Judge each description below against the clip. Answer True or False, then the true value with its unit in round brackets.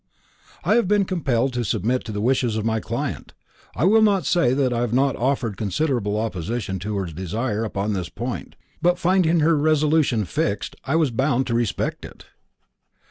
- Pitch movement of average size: False (6.3 semitones)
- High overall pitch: False (125 Hz)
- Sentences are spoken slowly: False (185 wpm)